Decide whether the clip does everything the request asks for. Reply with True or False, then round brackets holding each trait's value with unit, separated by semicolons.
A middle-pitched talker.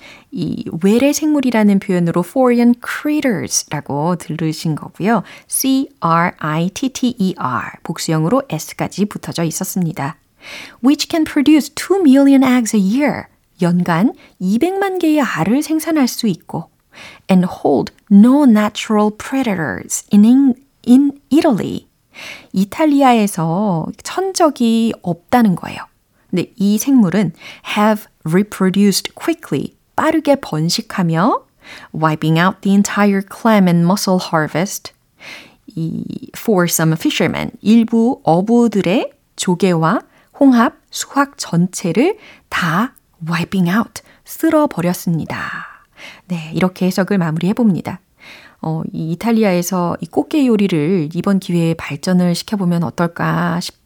False (205 Hz)